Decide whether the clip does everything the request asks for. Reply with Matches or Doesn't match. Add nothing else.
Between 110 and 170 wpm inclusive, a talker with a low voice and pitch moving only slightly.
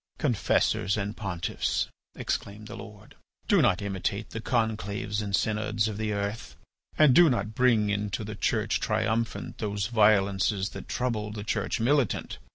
Matches